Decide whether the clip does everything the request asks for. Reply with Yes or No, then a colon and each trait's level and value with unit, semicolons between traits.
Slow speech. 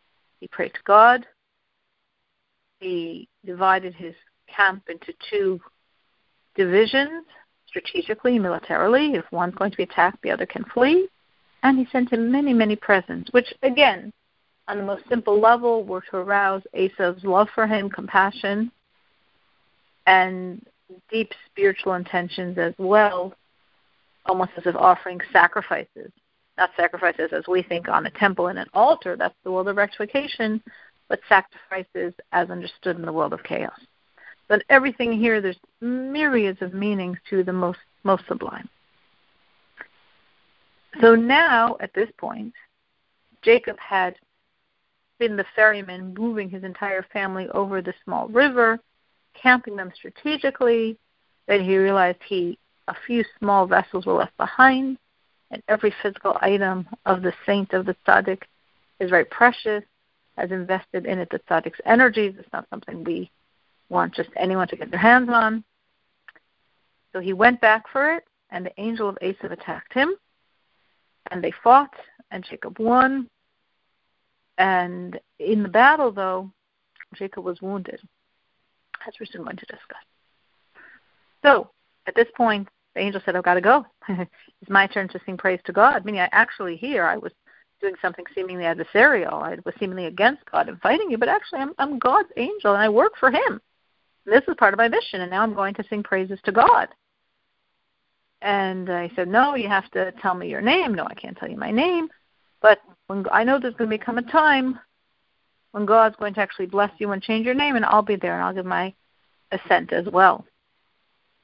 No: average, 165 wpm